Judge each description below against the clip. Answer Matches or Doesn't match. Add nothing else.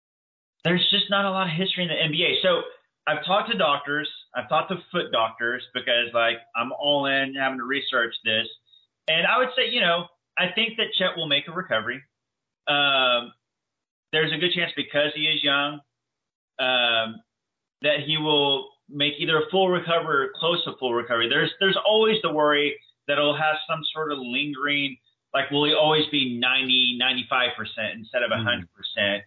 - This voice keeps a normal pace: Matches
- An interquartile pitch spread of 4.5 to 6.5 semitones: Matches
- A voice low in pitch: Doesn't match